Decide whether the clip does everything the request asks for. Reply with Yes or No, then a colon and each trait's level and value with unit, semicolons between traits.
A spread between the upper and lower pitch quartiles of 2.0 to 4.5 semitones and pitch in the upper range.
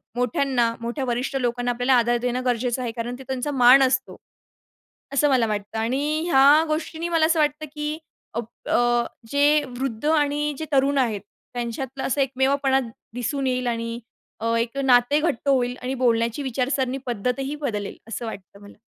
Yes: average, 2.9 semitones; very high, 255 Hz